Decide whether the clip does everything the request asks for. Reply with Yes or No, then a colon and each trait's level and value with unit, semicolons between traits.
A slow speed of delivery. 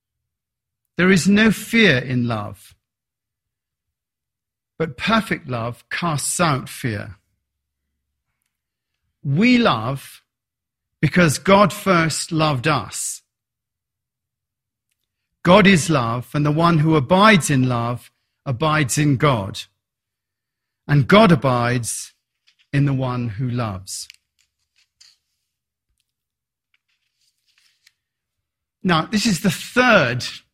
Yes: slow, 90 wpm